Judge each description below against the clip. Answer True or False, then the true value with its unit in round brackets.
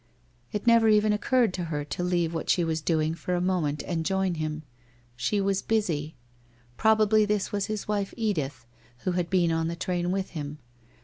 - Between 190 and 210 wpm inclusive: True (195 wpm)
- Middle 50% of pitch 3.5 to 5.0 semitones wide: True (4.4 semitones)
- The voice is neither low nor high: True (180 Hz)